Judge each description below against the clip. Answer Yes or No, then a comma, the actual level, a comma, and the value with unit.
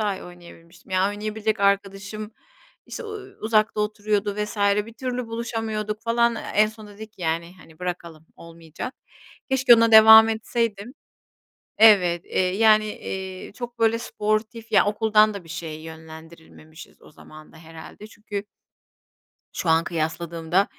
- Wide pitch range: No, average, 4.3 semitones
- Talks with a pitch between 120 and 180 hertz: No, high, 210 Hz